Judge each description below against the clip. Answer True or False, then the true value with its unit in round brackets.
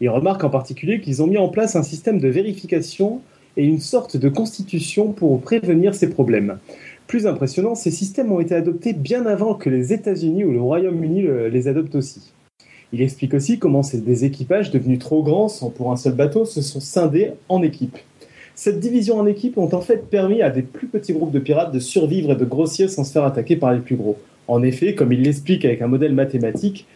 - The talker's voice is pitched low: False (160 Hz)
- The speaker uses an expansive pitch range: True (6.7 semitones)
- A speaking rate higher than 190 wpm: True (215 wpm)